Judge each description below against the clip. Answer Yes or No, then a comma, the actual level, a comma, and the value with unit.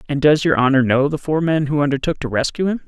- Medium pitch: Yes, medium, 150 Hz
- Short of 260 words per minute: No, fast, 270 wpm